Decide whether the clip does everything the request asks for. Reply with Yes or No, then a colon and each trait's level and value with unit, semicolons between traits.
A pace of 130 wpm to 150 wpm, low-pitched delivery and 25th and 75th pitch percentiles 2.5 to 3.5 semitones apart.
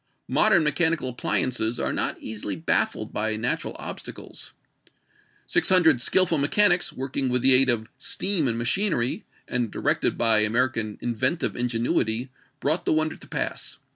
No: average, 140 wpm; low, 125 Hz; average, 5.3 semitones